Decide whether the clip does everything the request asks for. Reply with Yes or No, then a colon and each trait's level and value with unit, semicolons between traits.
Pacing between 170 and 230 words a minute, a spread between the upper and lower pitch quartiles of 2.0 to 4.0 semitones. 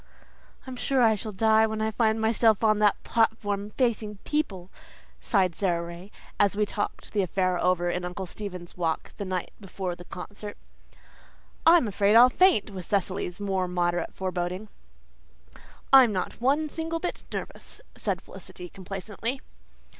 No: average, 155 wpm; average, 3.4 semitones